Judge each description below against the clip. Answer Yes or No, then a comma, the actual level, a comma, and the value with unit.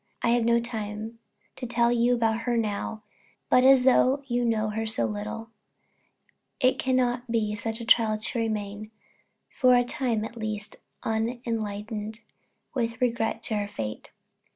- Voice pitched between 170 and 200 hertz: No, high, 230 Hz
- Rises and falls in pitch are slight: Yes, narrow, 2.1 semitones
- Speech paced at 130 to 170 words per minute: Yes, average, 150 wpm